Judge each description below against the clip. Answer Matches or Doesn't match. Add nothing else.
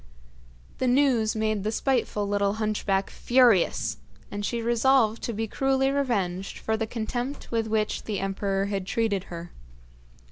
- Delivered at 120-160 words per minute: Matches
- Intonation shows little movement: Doesn't match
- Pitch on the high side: Matches